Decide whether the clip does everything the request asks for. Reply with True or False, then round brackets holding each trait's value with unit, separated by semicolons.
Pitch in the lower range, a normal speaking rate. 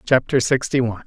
True (125 Hz; 170 wpm)